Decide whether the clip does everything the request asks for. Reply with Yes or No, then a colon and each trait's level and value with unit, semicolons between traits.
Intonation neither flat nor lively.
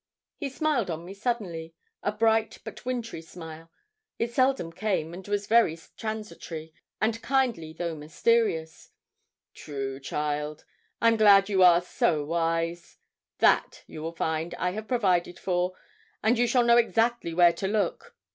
No: wide, 5.7 semitones